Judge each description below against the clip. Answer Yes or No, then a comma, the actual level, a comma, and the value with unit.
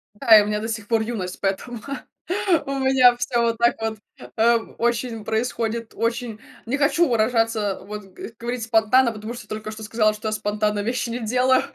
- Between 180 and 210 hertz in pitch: No, high, 225 Hz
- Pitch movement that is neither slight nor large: No, narrow, 1.9 semitones